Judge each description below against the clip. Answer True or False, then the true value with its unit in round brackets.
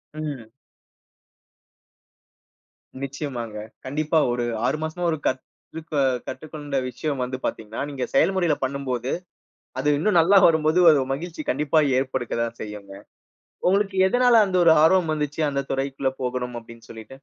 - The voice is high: False (140 Hz)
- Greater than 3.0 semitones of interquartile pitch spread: True (4.0 semitones)